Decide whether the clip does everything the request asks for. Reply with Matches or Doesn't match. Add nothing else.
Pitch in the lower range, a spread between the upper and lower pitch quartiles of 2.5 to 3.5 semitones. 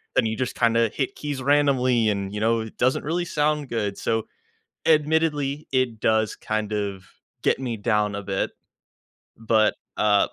Doesn't match